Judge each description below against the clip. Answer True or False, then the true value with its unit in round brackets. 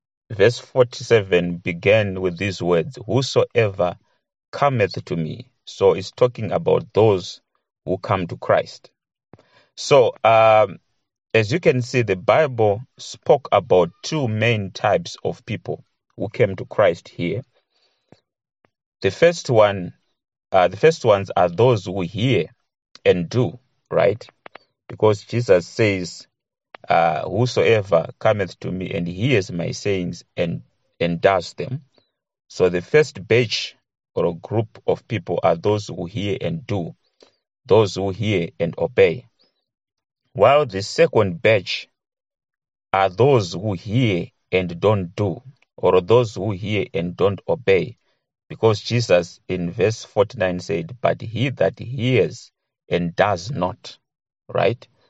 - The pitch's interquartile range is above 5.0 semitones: True (5.5 semitones)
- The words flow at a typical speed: False (130 wpm)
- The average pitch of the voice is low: True (110 Hz)